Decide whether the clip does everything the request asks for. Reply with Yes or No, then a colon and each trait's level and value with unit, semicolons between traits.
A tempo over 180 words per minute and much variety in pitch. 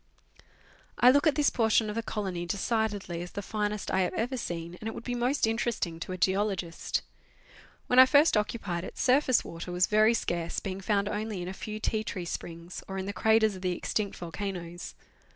No: fast, 205 wpm; average, 3.8 semitones